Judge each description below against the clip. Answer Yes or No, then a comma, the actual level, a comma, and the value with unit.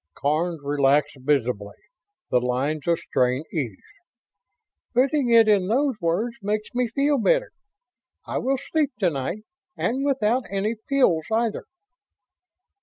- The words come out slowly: Yes, slow, 125 wpm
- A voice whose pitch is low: No, high, 200 Hz